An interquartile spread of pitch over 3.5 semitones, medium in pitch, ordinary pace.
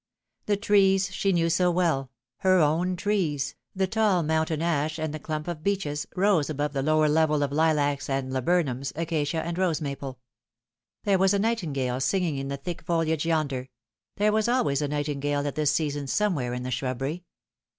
Yes: average, 4.1 semitones; medium, 155 Hz; average, 180 wpm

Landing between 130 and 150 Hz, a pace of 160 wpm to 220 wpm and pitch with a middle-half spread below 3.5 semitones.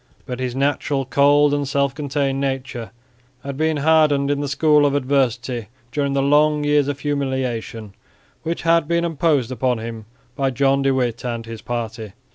Yes: medium, 140 Hz; average, 170 wpm; narrow, 2.6 semitones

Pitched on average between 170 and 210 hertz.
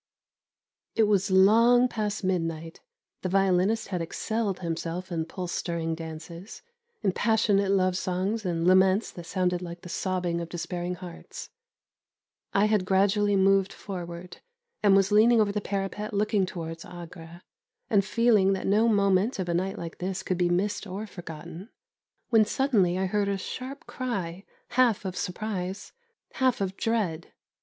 Yes: high, 190 Hz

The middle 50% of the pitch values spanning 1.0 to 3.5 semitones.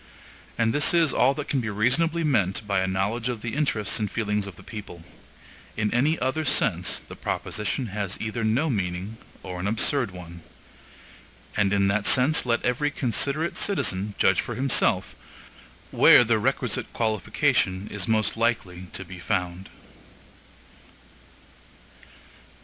No: average, 4.7 semitones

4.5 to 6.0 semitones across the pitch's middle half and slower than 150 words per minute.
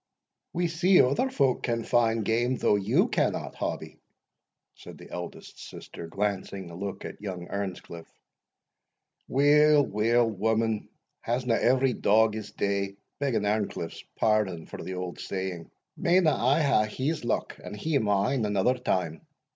Yes: average, 4.8 semitones; average, 140 wpm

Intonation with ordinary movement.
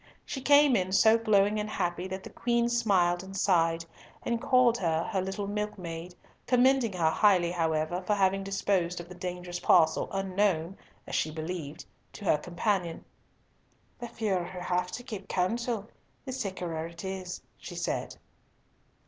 Yes: average, 3.3 semitones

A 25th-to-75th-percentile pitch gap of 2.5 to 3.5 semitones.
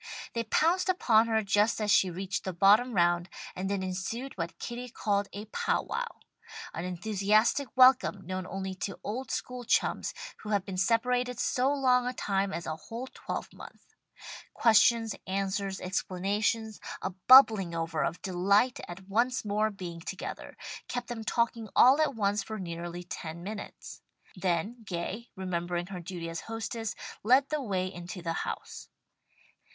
No: average, 4.2 semitones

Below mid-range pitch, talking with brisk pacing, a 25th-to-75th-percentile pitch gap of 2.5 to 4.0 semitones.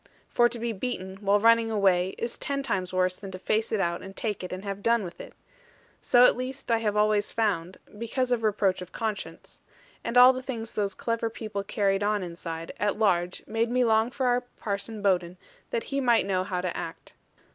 No: high, 210 Hz; fast, 210 wpm; average, 3.6 semitones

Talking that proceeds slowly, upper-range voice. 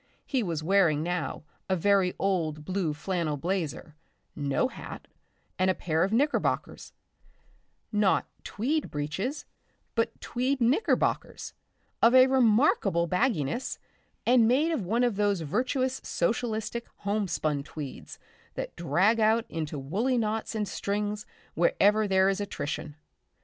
Yes: slow, 125 wpm; high, 200 Hz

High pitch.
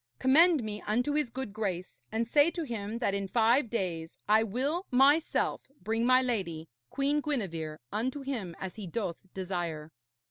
Yes: high, 225 Hz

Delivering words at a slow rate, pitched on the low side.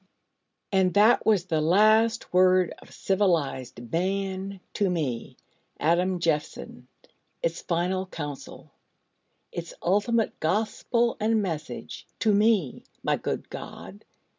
No: slow, 110 wpm; medium, 185 Hz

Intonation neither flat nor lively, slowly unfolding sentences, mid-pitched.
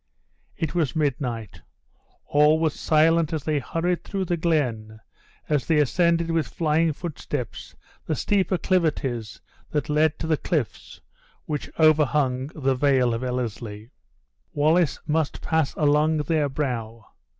Yes: average, 3.7 semitones; slow, 130 wpm; medium, 150 Hz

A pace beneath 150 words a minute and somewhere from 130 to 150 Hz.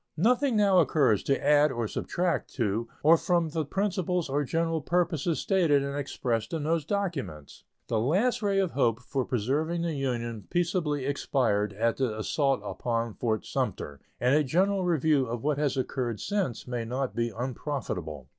No: average, 165 wpm; medium, 140 Hz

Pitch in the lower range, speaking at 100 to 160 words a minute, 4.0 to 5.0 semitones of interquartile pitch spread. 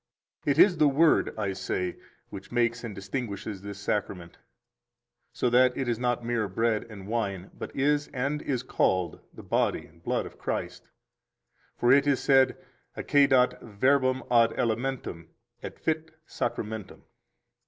Yes: low, 120 Hz; average, 150 wpm; average, 4.7 semitones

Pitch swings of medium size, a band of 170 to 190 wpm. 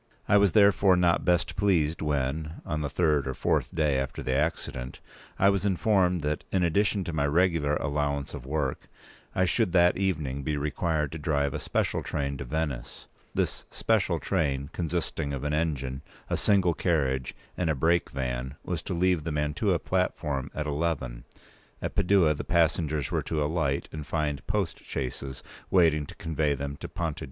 Yes: average, 3.5 semitones; average, 180 wpm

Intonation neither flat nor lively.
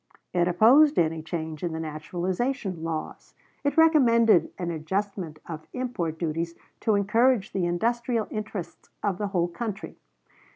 No: wide, 5.7 semitones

